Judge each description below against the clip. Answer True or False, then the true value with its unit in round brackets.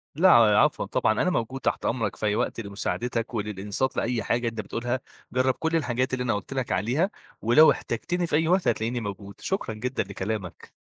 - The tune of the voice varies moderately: True (3.5 semitones)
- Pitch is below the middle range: True (120 Hz)